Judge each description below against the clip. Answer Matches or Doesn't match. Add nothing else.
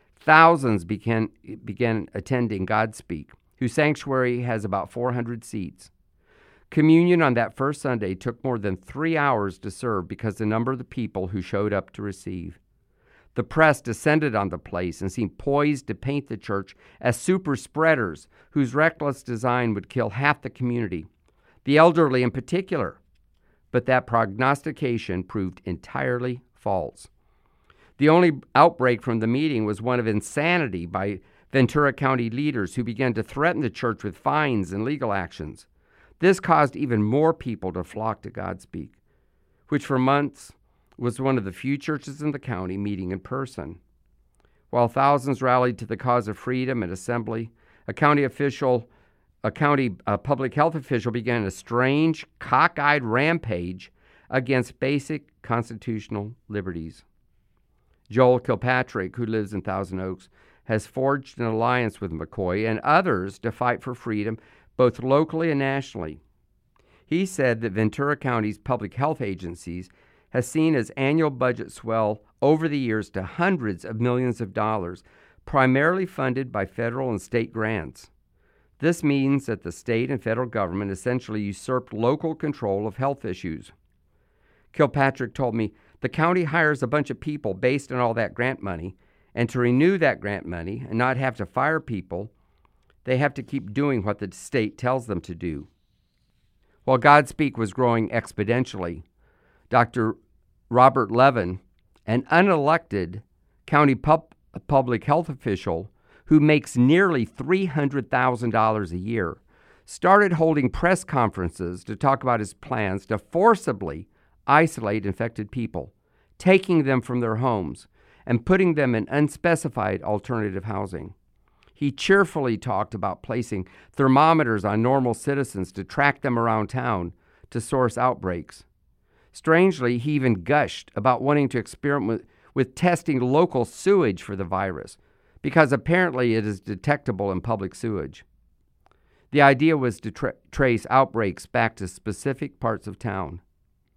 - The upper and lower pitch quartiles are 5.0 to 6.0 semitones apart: Matches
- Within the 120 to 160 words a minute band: Matches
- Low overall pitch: Matches